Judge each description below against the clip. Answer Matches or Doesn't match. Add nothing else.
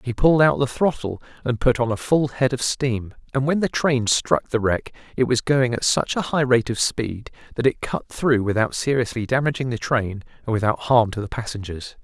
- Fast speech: Matches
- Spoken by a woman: Doesn't match